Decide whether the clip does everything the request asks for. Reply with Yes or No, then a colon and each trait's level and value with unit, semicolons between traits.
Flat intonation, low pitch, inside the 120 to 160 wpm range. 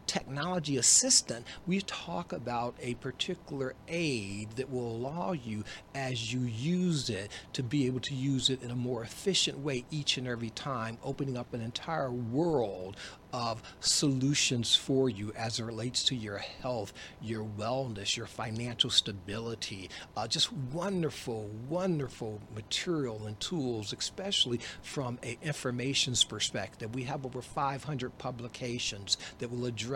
No: average, 3.8 semitones; low, 125 Hz; average, 140 wpm